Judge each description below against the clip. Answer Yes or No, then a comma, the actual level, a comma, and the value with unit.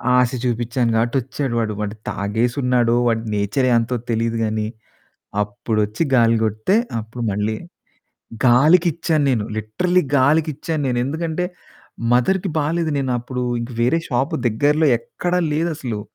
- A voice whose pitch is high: No, low, 125 Hz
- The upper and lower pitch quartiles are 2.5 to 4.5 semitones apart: No, average, 5.1 semitones